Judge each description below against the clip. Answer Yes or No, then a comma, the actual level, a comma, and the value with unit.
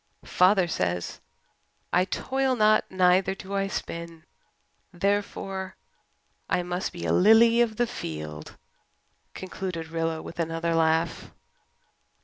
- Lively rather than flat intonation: No, average, 3.2 semitones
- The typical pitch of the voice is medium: Yes, medium, 180 Hz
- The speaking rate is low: Yes, slow, 115 wpm